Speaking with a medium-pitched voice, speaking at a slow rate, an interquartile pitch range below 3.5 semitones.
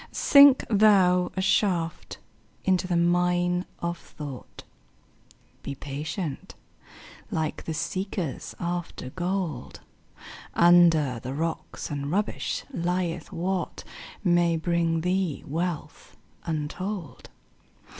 Yes: medium, 175 Hz; slow, 95 wpm; narrow, 2.4 semitones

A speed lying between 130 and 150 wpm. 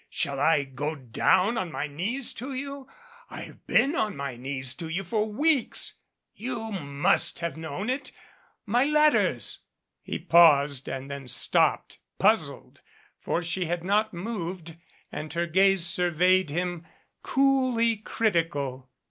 Yes: average, 140 wpm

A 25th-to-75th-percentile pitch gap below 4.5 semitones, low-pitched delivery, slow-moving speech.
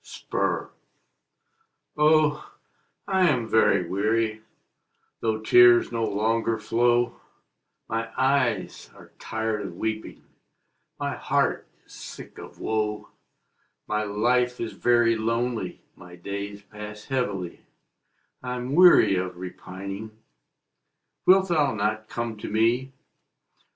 Yes: average, 2.7 semitones; low, 110 Hz; slow, 105 wpm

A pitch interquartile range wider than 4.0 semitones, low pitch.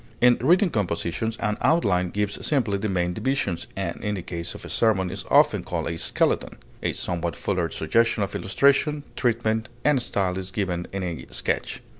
Yes: average, 4.7 semitones; low, 100 Hz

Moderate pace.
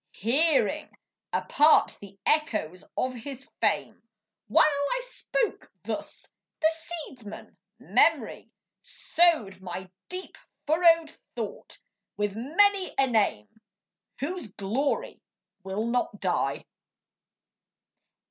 No: slow, 90 wpm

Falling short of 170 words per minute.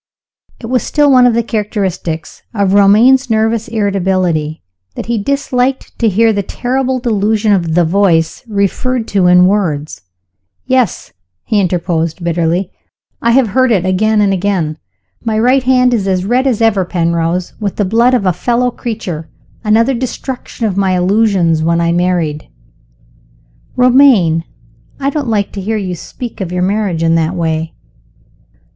Yes: average, 155 wpm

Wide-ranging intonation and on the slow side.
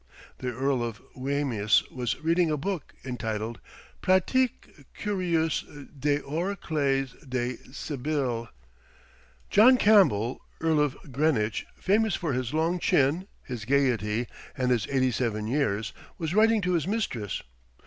Yes: wide, 5.8 semitones; slow, 125 wpm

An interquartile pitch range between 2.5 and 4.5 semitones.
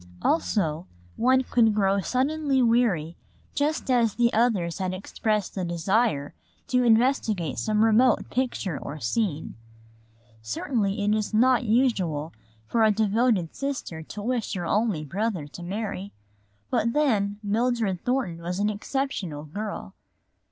No: average, 5.2 semitones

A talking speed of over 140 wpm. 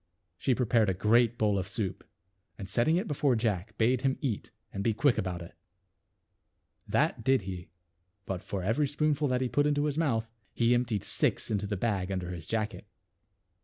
Yes: average, 200 wpm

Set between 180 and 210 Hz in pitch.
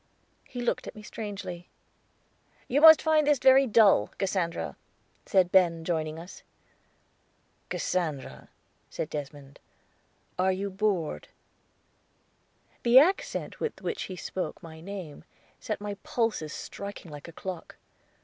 Yes: high, 190 Hz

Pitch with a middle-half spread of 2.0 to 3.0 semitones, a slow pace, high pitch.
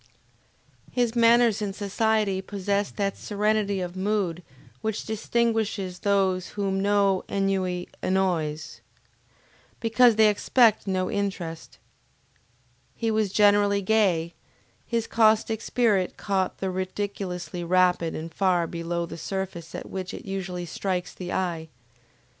Yes: average, 2.7 semitones; slow, 120 wpm; high, 195 Hz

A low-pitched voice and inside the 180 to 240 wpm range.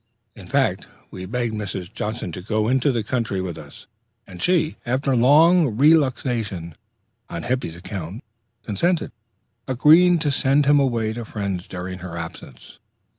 No: low, 115 Hz; average, 145 wpm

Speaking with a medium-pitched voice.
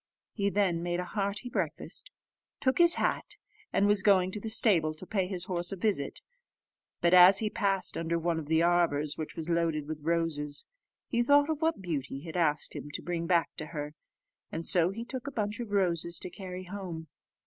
Yes: medium, 180 Hz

